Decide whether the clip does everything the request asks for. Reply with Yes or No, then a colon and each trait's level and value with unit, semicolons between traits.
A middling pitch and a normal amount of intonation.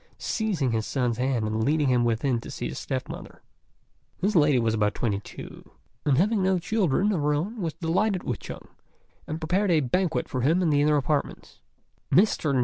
No: medium, 150 Hz; wide, 6.5 semitones